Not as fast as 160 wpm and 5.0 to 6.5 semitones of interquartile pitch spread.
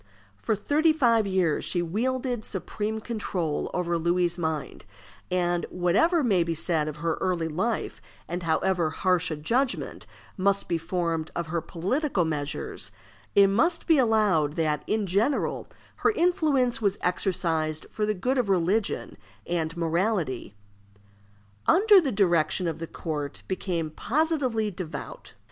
Yes: slow, 135 wpm; wide, 5.4 semitones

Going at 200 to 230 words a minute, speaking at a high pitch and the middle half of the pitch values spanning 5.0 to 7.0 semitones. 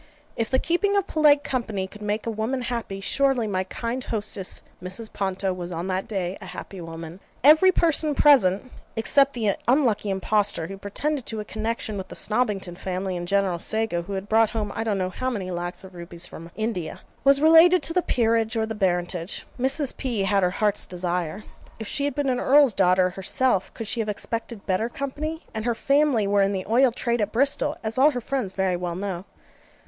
Yes: fast, 205 wpm; high, 215 Hz; average, 5.3 semitones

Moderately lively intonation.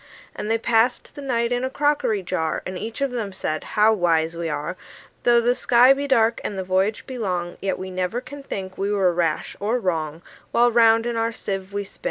Yes: average, 4.5 semitones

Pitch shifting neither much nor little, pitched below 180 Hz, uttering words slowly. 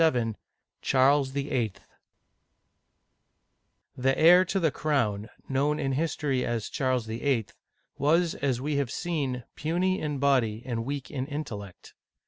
Yes: average, 3.5 semitones; low, 135 Hz; slow, 125 wpm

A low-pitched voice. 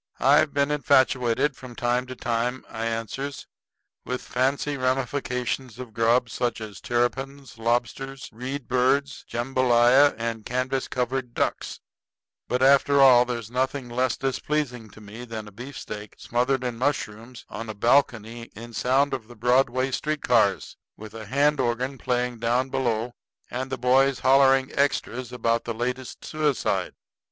Yes: low, 125 Hz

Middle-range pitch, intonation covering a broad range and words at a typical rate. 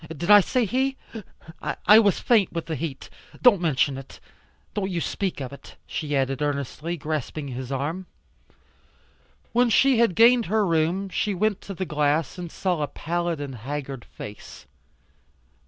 Yes: medium, 165 Hz; wide, 5.9 semitones; average, 160 wpm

